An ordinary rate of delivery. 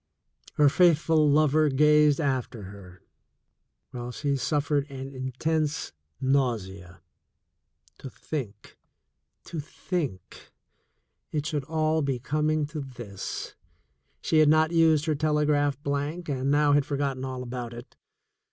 No: slow, 130 wpm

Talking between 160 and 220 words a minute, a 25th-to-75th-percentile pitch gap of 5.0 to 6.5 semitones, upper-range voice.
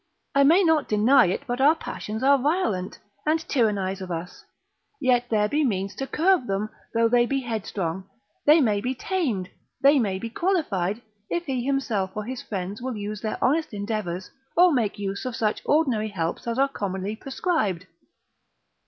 Yes: average, 175 wpm; wide, 5.6 semitones; high, 230 Hz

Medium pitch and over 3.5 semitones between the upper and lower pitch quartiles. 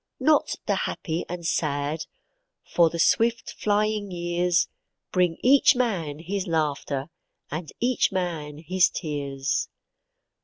Yes: medium, 175 Hz; average, 4.6 semitones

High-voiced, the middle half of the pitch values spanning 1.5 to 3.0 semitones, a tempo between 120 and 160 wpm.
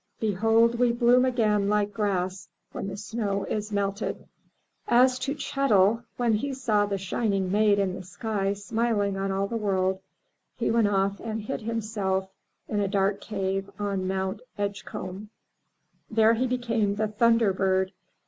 Yes: high, 205 Hz; average, 2.7 semitones; average, 155 wpm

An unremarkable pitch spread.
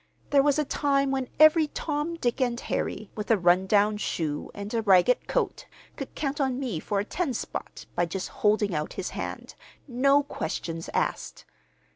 No: wide, 6.3 semitones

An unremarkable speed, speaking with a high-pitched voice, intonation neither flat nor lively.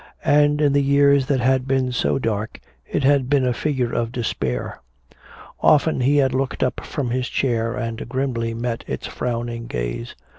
No: average, 175 wpm; low, 130 Hz; average, 3.0 semitones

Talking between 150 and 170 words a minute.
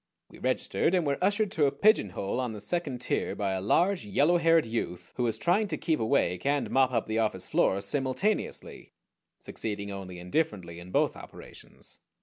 No: average, 180 wpm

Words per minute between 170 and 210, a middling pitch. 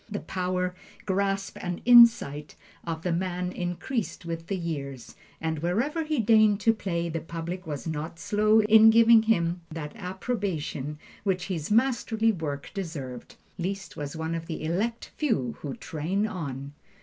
No: average, 150 wpm; medium, 180 Hz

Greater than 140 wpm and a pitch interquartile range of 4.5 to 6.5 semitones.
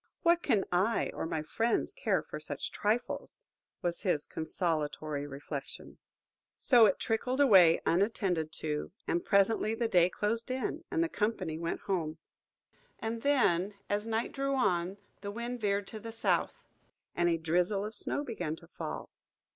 Yes: average, 160 wpm; average, 5.3 semitones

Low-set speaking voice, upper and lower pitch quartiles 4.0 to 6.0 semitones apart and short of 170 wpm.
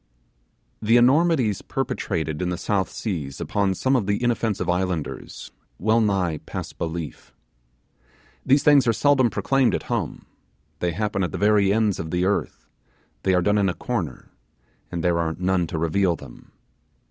Yes: very low, 95 Hz; average, 4.6 semitones; average, 160 wpm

